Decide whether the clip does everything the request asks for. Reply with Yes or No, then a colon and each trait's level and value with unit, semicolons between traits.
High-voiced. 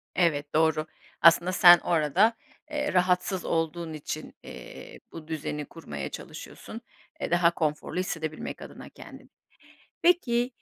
No: medium, 170 Hz